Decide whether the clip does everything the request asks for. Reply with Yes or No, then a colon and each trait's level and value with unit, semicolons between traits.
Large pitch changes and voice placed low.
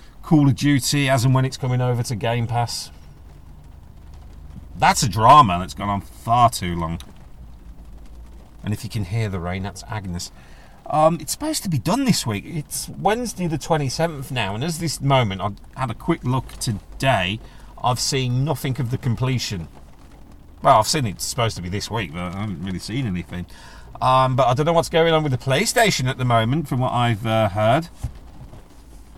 Yes: wide, 7.5 semitones; low, 115 Hz